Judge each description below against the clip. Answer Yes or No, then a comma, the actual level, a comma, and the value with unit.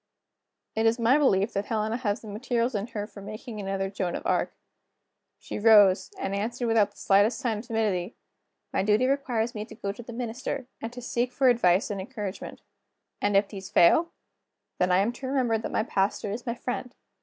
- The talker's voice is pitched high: Yes, high, 220 Hz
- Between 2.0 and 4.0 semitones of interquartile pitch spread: Yes, average, 3.2 semitones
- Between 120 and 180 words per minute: No, average, 200 wpm